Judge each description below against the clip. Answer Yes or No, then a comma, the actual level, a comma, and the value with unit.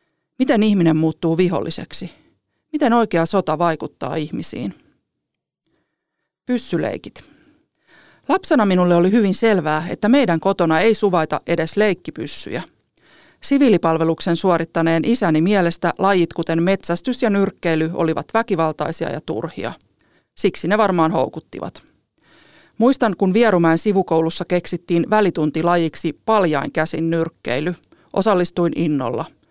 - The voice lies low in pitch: No, medium, 175 Hz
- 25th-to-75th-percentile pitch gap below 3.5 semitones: No, average, 4.2 semitones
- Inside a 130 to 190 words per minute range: No, average, 100 wpm